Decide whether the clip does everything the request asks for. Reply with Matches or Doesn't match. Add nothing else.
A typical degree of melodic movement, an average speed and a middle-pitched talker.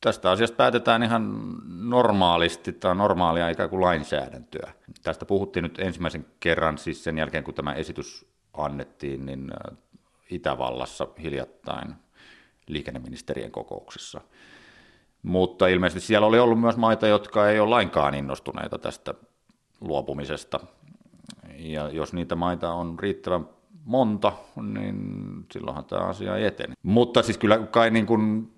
Doesn't match